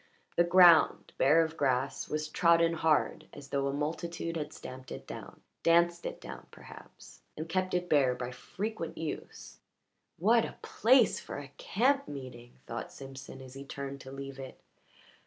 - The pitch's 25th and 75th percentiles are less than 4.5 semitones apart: Yes, average, 4.0 semitones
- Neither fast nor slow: Yes, average, 165 wpm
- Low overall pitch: No, medium, 155 Hz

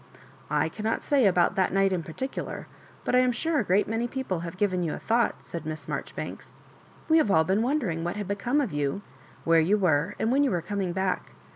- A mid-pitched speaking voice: No, high, 195 Hz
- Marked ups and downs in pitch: Yes, wide, 5.8 semitones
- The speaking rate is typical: No, fast, 235 wpm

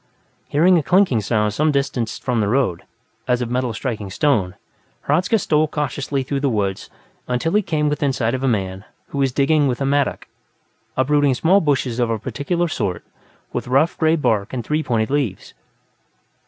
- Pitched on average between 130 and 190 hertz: Yes, low, 135 Hz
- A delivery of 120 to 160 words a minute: No, average, 180 wpm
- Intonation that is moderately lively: Yes, average, 4.5 semitones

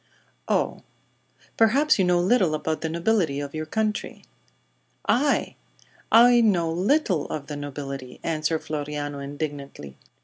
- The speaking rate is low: Yes, slow, 125 wpm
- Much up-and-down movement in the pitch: Yes, wide, 6.5 semitones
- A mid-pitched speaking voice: Yes, medium, 160 Hz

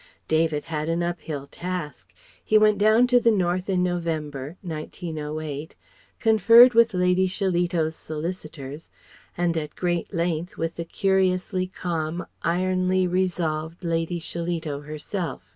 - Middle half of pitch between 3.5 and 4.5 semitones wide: No, average, 2.8 semitones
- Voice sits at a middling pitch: Yes, medium, 175 Hz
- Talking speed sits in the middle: No, slow, 125 wpm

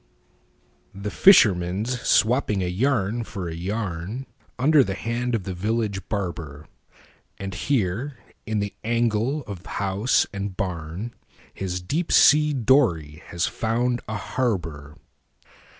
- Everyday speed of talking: No, slow, 110 wpm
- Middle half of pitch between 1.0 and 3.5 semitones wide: No, average, 5.0 semitones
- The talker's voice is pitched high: No, low, 105 Hz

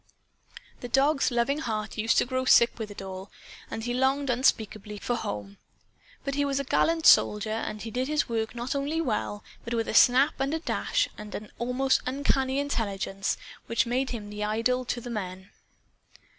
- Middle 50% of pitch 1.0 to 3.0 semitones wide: No, average, 4.1 semitones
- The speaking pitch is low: No, high, 240 Hz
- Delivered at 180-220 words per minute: Yes, average, 185 wpm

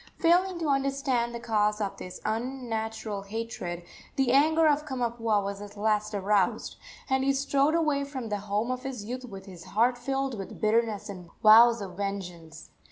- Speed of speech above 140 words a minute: Yes, average, 170 wpm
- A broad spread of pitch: No, average, 4.8 semitones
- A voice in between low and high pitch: No, high, 230 Hz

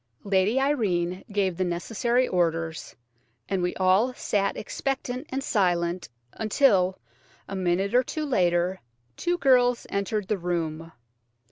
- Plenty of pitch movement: Yes, wide, 5.7 semitones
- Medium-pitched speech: No, high, 195 Hz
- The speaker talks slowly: Yes, slow, 125 wpm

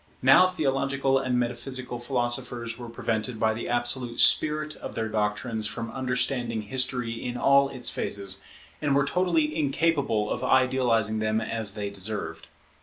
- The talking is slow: No, average, 145 wpm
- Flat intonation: No, average, 3.3 semitones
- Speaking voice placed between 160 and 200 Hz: No, low, 125 Hz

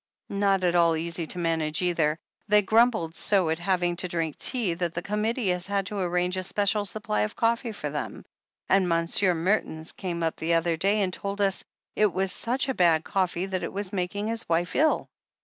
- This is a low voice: No, medium, 185 Hz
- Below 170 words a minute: No, fast, 205 wpm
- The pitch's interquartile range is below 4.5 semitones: Yes, average, 3.3 semitones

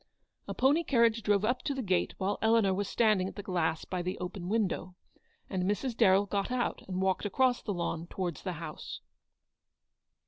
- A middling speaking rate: Yes, average, 185 wpm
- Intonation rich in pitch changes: No, average, 3.8 semitones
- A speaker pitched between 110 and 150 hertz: No, high, 200 Hz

